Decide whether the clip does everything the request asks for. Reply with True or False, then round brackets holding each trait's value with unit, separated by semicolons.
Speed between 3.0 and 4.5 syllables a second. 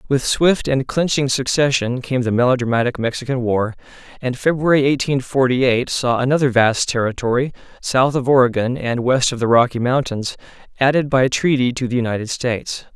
False (5.4 syllables/s)